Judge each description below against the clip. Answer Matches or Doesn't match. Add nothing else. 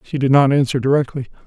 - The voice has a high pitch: Doesn't match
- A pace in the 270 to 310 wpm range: Doesn't match